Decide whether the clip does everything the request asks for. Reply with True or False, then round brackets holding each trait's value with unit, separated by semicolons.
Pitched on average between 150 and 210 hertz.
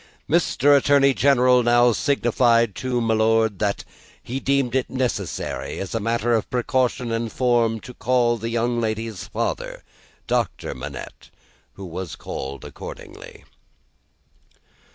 False (120 Hz)